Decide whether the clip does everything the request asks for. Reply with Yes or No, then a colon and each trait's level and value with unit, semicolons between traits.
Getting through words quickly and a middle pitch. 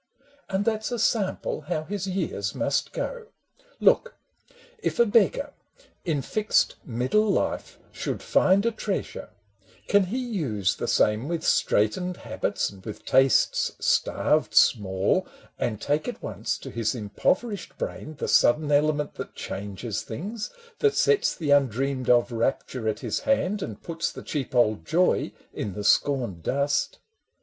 No: average, 150 wpm; medium, 150 Hz